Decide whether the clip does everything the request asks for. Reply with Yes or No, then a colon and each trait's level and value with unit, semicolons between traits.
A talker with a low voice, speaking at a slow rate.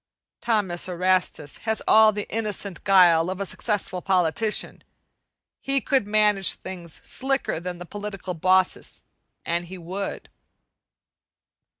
No: high, 190 Hz; slow, 115 wpm